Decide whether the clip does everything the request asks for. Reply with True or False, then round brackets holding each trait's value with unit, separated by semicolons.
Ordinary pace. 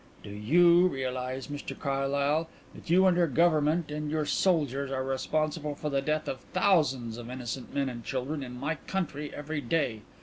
True (175 wpm)